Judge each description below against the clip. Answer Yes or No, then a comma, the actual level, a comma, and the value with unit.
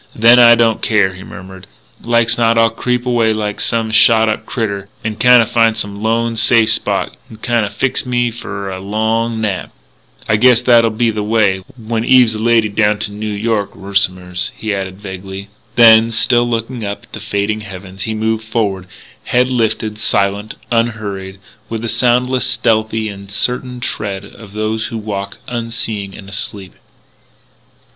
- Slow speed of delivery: No, average, 165 wpm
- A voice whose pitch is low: Yes, low, 110 Hz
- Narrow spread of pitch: Yes, narrow, 2.3 semitones